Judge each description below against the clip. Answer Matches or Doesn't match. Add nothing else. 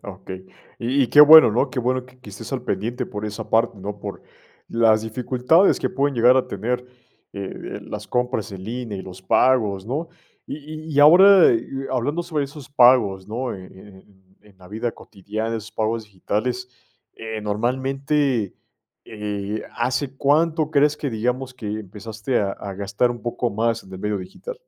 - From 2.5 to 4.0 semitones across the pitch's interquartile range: Doesn't match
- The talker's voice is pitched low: Matches